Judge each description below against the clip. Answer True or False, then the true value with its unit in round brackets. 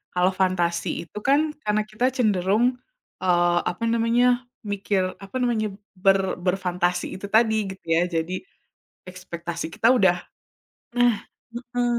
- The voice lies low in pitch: False (195 Hz)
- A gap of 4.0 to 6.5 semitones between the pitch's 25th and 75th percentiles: True (4.5 semitones)